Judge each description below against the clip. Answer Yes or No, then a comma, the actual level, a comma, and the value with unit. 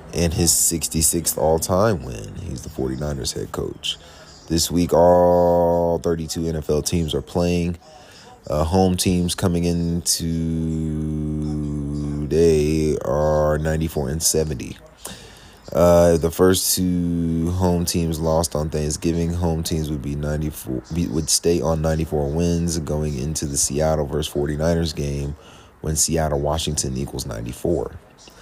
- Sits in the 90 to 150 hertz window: No, very low, 80 Hz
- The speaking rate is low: Yes, slow, 125 wpm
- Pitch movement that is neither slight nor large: No, narrow, 2.2 semitones